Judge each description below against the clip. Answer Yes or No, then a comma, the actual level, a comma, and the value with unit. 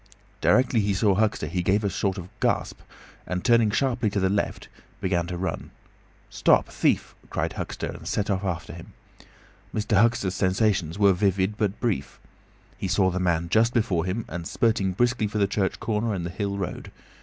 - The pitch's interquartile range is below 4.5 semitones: Yes, average, 2.8 semitones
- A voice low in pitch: Yes, low, 100 Hz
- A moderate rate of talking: Yes, average, 185 wpm